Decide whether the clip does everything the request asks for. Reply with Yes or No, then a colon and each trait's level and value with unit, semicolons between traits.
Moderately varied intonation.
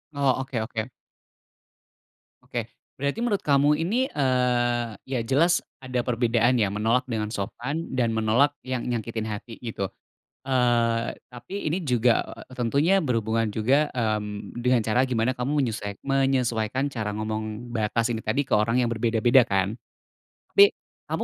Yes: average, 3.2 semitones